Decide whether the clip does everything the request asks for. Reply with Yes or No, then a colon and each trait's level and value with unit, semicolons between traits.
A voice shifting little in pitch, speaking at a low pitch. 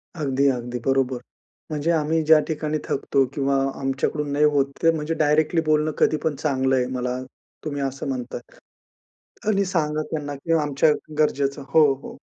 No: narrow, 2.3 semitones; medium, 145 Hz